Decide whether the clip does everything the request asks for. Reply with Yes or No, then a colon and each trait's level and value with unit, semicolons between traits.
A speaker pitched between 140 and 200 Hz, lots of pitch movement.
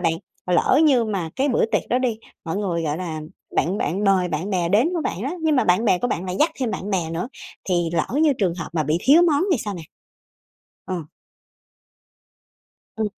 Yes: high, 190 Hz; wide, 6.3 semitones